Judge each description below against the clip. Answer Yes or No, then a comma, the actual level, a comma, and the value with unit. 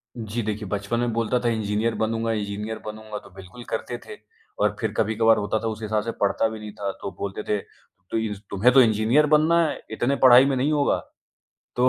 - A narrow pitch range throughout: Yes, narrow, 2.3 semitones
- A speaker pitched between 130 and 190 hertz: No, low, 110 Hz